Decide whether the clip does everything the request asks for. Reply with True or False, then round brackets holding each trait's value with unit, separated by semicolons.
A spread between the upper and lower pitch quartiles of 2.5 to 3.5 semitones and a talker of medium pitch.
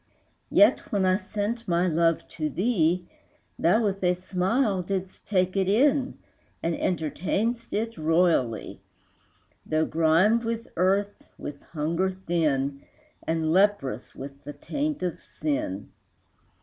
False (4.3 semitones; 180 Hz)